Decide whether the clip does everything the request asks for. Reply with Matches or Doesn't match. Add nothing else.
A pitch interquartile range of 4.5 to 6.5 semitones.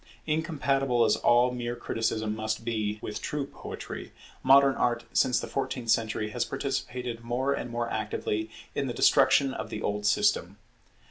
Doesn't match